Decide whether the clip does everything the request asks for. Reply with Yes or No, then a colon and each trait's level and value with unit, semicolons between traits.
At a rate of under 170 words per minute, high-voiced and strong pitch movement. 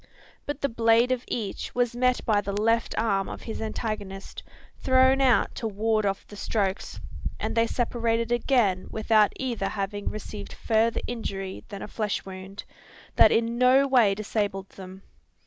No: average, 160 wpm; high, 220 Hz; average, 3.1 semitones